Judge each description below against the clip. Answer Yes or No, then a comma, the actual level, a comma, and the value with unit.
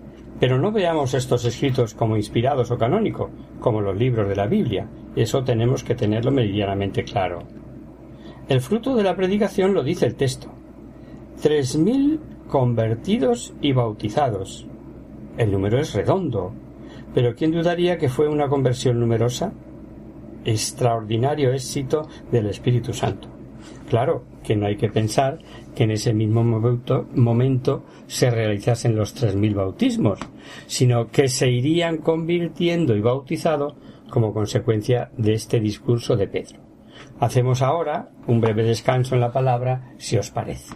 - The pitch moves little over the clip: No, average, 4.0 semitones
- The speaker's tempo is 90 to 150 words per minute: Yes, average, 140 wpm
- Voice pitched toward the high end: No, low, 125 Hz